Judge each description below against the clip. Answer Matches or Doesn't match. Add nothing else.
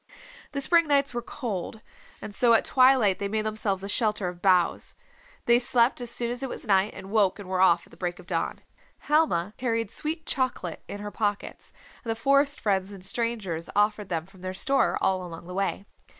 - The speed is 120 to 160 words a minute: Doesn't match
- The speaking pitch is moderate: Doesn't match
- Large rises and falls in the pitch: Doesn't match